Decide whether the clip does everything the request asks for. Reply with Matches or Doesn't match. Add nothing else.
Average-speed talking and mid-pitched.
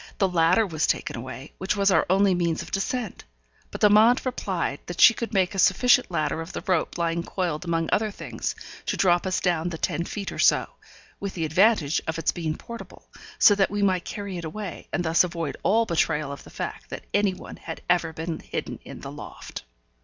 Doesn't match